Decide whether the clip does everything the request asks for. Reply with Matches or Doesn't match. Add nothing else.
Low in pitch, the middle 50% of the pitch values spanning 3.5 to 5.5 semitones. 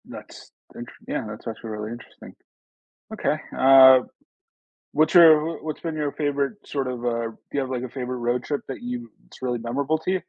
Matches